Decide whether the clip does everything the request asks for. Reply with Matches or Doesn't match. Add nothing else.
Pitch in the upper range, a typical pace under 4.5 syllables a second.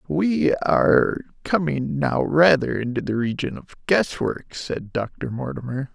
Doesn't match